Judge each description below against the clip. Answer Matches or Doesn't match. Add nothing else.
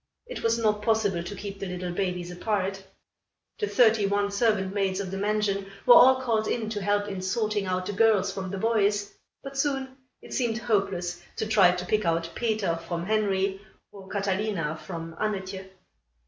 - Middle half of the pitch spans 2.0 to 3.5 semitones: Matches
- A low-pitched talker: Doesn't match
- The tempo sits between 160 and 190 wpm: Matches